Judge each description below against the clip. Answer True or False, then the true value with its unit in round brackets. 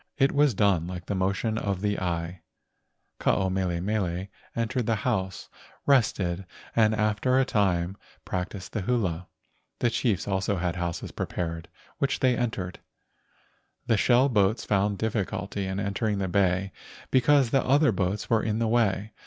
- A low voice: True (100 Hz)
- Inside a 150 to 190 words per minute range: True (155 wpm)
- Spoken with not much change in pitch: False (3.6 semitones)